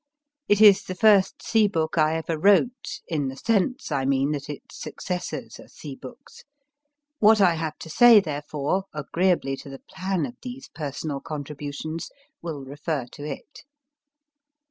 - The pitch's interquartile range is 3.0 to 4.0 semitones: No, wide, 5.4 semitones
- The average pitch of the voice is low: No, medium, 160 Hz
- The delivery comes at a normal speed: Yes, average, 155 wpm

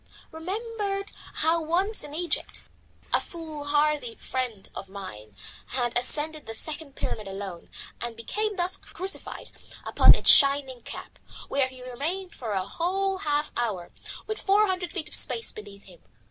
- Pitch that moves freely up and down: Yes, wide, 7.5 semitones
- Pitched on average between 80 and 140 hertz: No, very high, 295 Hz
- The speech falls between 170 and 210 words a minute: No, average, 145 wpm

